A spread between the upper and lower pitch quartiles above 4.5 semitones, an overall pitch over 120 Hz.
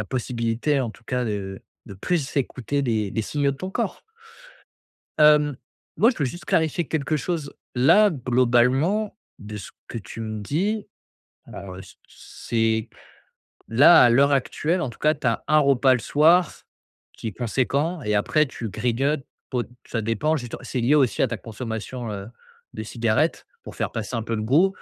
Yes: average, 5.1 semitones; low, 130 Hz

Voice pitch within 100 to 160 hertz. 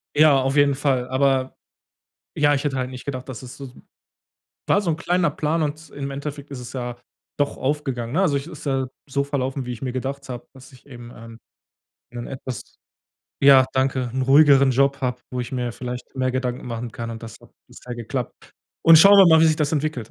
Yes: low, 135 Hz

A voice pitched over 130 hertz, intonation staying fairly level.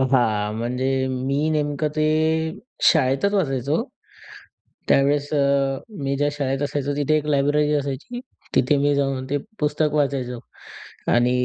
Yes: medium, 140 Hz; narrow, 1.9 semitones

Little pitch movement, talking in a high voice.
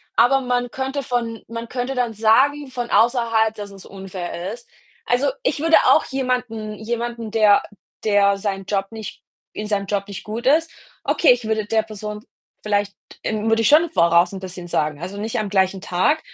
No: average, 3.6 semitones; high, 220 Hz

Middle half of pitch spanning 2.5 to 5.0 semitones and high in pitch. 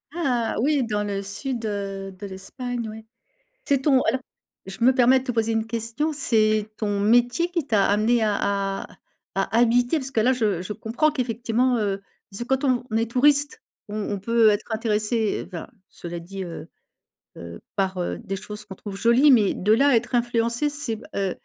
Yes: average, 3.5 semitones; high, 225 Hz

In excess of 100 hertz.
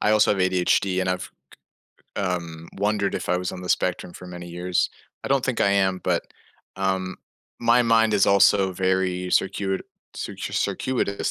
No: very low, 95 Hz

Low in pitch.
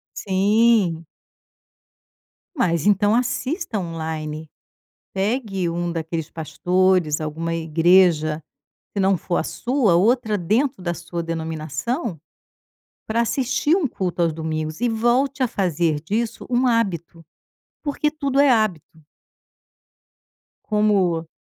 No: medium, 185 Hz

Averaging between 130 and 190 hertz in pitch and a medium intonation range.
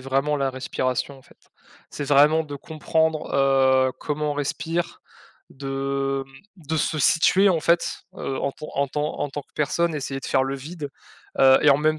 No: medium, 140 Hz; narrow, 2.3 semitones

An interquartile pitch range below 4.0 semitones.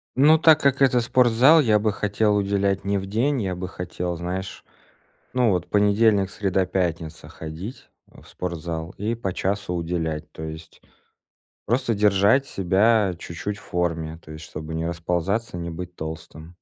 No: average, 4.4 semitones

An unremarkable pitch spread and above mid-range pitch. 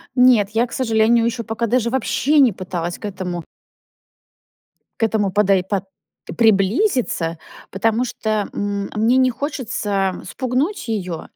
Yes: average, 4.1 semitones; high, 220 Hz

